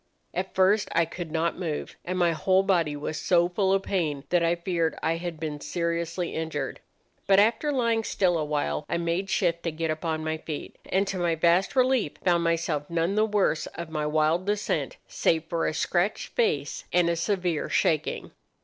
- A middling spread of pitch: Yes, average, 3.0 semitones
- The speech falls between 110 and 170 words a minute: No, average, 190 wpm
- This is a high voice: No, medium, 170 Hz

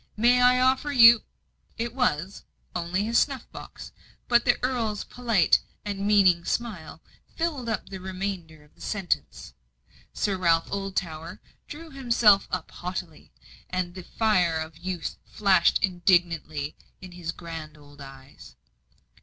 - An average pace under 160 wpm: Yes, slow, 135 wpm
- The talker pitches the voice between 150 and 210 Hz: Yes, high, 190 Hz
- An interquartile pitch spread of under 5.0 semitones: No, wide, 5.6 semitones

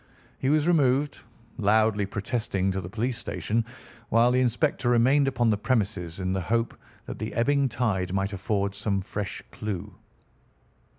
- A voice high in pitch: No, low, 110 Hz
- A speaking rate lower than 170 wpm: Yes, average, 155 wpm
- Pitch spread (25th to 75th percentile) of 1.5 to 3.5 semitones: No, average, 4.1 semitones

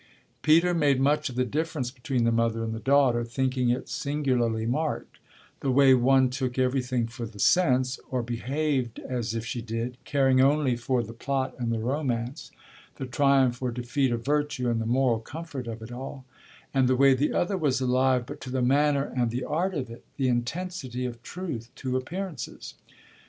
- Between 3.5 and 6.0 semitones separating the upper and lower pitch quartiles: No, average, 2.8 semitones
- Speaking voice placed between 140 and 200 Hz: No, low, 130 Hz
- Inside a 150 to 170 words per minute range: No, average, 190 wpm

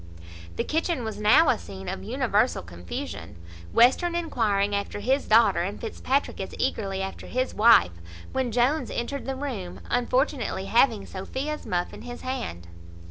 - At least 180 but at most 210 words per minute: No, average, 150 wpm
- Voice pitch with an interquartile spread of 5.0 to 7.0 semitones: Yes, wide, 5.4 semitones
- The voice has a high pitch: Yes, high, 230 Hz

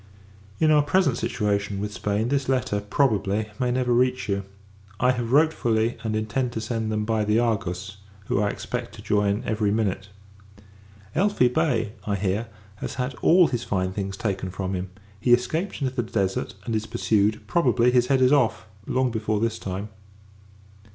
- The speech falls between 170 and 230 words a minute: Yes, average, 180 wpm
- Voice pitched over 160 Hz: No, low, 110 Hz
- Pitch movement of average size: Yes, average, 3.6 semitones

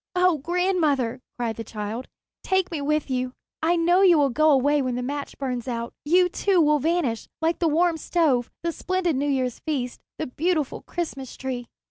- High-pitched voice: Yes, very high, 295 Hz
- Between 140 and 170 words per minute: No, average, 185 wpm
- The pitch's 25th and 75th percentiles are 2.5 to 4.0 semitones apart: No, average, 5.2 semitones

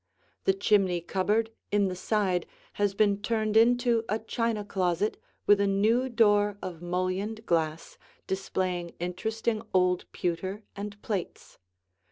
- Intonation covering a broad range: No, average, 3.0 semitones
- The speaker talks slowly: Yes, slow, 130 wpm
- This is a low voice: No, high, 200 Hz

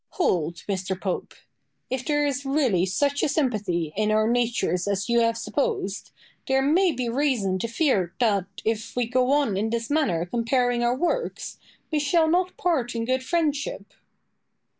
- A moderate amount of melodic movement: No, wide, 5.7 semitones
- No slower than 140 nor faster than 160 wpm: No, average, 170 wpm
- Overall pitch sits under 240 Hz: No, high, 245 Hz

